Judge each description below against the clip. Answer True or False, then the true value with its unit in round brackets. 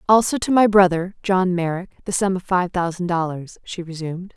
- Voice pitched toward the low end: False (185 Hz)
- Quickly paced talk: False (195 wpm)